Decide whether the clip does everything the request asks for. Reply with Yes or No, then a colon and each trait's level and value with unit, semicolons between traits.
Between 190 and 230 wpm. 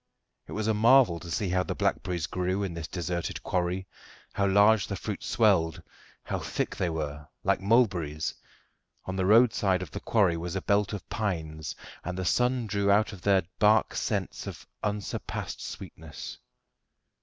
No: average, 170 wpm